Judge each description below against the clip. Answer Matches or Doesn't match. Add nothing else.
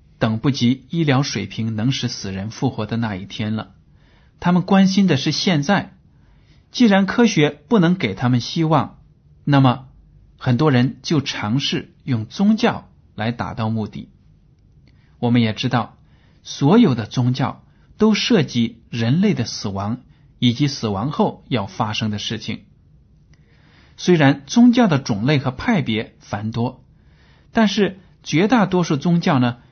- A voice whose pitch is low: Matches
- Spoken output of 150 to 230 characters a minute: Matches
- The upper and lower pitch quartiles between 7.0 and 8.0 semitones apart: Doesn't match